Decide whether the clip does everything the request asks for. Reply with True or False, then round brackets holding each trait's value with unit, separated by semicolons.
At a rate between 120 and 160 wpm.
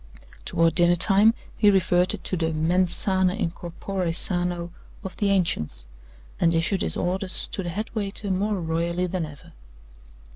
True (155 wpm)